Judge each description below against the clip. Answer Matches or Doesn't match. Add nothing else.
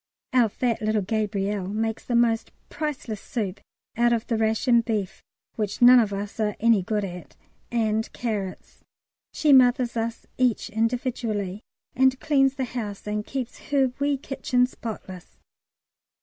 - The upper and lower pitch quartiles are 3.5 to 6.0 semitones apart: Doesn't match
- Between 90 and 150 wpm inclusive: Matches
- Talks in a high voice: Matches